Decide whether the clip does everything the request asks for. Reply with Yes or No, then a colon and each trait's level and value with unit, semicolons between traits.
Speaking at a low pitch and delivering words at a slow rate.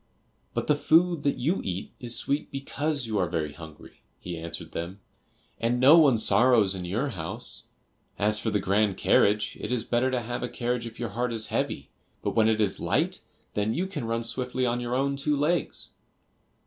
No: low, 120 Hz; average, 200 wpm